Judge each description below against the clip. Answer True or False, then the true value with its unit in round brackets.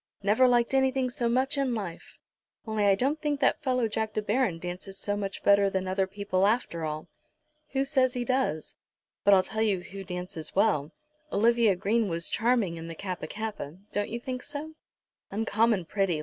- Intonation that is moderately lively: True (4.8 semitones)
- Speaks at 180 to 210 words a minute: True (185 wpm)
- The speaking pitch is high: True (210 Hz)